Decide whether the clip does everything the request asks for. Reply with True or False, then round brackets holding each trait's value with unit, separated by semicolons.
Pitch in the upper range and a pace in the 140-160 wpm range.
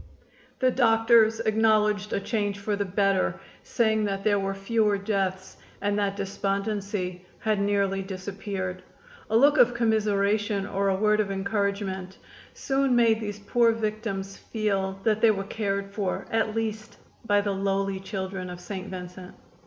True (205 Hz; 150 wpm)